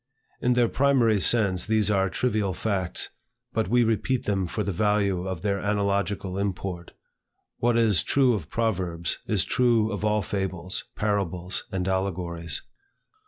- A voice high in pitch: No, low, 100 Hz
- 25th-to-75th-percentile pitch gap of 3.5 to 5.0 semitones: No, average, 3.0 semitones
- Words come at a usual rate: Yes, average, 145 wpm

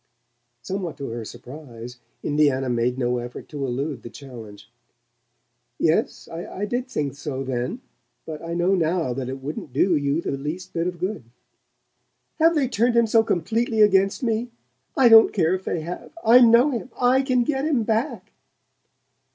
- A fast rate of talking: No, average, 165 wpm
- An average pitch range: No, wide, 9.0 semitones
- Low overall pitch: No, medium, 170 Hz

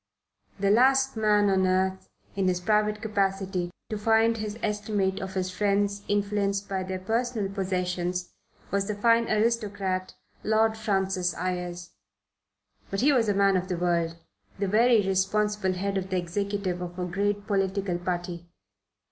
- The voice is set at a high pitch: Yes, high, 195 Hz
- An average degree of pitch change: No, narrow, 2.2 semitones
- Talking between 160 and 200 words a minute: No, average, 150 wpm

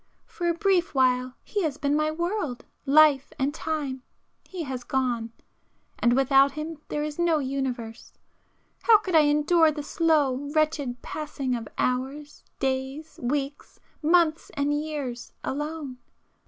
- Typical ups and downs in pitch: Yes, average, 3.0 semitones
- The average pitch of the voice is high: Yes, very high, 290 Hz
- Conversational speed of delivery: No, slow, 130 wpm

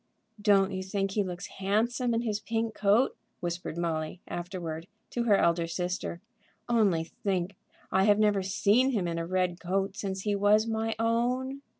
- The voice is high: Yes, high, 195 Hz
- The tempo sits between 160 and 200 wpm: Yes, average, 170 wpm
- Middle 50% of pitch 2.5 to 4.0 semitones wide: Yes, average, 3.7 semitones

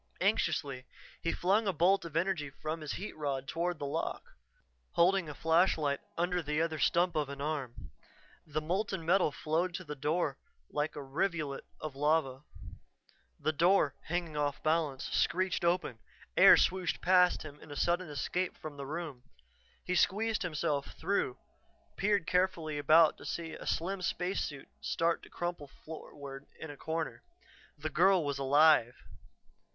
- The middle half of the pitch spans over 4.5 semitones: No, average, 3.4 semitones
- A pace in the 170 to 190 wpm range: No, average, 155 wpm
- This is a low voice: No, medium, 160 Hz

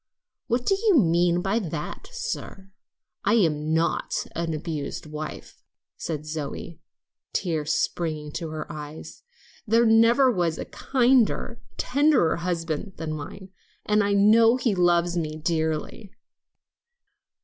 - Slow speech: Yes, slow, 125 wpm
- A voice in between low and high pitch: Yes, medium, 175 Hz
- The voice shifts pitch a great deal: Yes, wide, 6.2 semitones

